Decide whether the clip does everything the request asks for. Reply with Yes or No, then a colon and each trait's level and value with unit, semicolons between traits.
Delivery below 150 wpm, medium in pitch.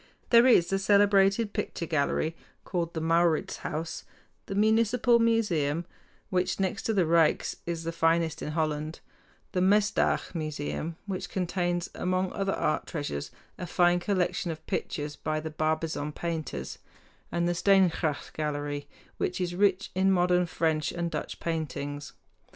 Yes: average, 140 wpm; medium, 170 Hz